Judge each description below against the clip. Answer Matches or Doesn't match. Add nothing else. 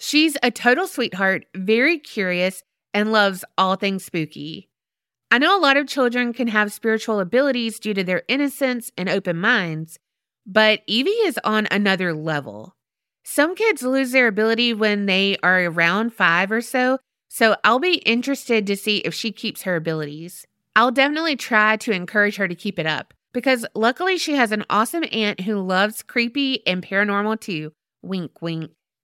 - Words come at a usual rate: Matches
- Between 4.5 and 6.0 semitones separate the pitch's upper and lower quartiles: Matches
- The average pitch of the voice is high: Matches